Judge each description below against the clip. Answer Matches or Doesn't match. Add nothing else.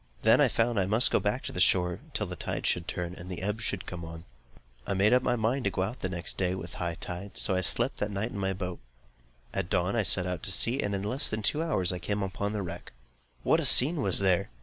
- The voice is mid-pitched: Doesn't match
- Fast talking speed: Matches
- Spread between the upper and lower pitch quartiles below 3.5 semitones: Matches